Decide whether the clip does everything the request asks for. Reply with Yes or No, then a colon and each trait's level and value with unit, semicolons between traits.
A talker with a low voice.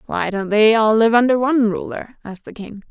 No: high, 220 Hz